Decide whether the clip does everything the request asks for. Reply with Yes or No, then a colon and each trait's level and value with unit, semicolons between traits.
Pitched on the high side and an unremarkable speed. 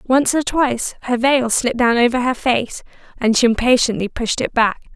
Yes: high, 245 Hz; average, 195 wpm